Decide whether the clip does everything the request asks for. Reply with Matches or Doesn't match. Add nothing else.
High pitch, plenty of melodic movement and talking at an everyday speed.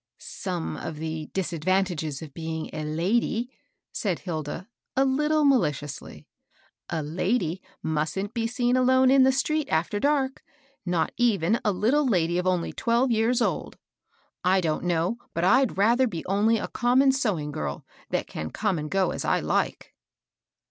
Matches